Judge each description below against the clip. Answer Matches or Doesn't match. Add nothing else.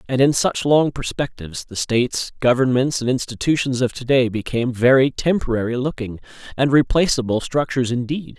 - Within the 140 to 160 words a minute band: Matches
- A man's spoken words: Matches